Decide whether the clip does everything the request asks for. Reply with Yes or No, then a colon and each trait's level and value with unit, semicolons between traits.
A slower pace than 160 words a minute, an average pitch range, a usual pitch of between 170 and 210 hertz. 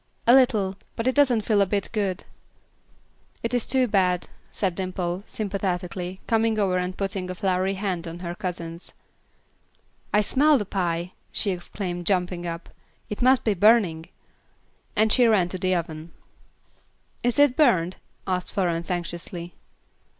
Yes: average, 150 wpm; average, 3.5 semitones; high, 190 Hz